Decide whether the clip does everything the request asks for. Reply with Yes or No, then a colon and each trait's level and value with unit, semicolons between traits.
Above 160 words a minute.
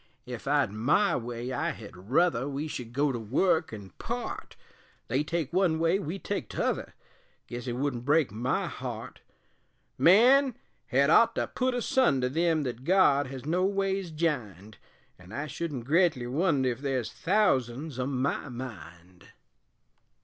No: average, 150 wpm